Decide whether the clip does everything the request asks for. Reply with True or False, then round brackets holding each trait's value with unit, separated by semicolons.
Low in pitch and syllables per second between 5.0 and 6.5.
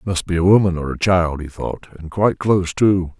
True (90 Hz; 5.6 syllables/s)